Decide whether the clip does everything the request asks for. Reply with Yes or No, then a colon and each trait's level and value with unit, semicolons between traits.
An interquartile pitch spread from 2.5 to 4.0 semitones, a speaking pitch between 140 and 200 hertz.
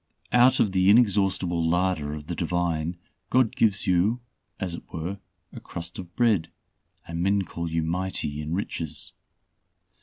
No: average, 3.0 semitones; very low, 90 Hz